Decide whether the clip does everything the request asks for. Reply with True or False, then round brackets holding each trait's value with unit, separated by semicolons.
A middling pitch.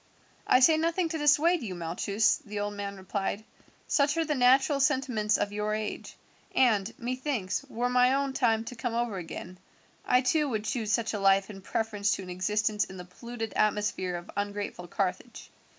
False (220 Hz)